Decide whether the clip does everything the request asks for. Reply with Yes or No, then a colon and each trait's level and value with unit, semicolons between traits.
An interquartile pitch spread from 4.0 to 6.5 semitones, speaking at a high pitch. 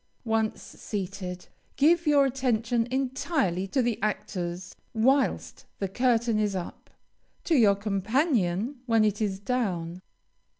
Yes: average, 4.9 semitones; high, 220 Hz